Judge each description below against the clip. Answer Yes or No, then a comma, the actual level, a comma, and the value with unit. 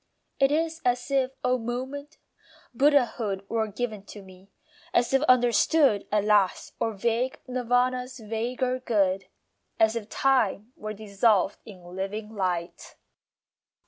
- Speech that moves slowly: Yes, slow, 125 wpm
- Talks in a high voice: Yes, high, 230 Hz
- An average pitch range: Yes, average, 3.7 semitones